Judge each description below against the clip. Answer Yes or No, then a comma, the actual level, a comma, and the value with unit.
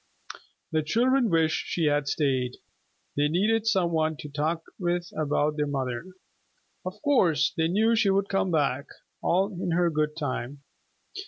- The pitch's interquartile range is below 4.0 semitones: No, average, 4.3 semitones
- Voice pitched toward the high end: No, medium, 160 Hz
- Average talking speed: Yes, average, 155 wpm